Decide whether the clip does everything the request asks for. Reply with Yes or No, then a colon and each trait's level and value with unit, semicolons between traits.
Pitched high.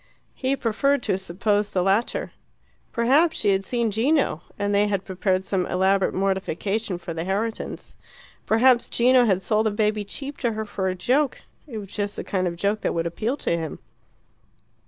Yes: high, 205 Hz